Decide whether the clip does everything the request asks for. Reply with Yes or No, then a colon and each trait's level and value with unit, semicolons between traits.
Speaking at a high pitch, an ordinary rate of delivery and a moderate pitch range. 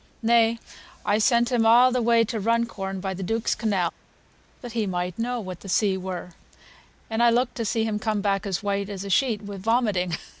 No: high, 215 Hz; fast, 210 wpm; average, 3.2 semitones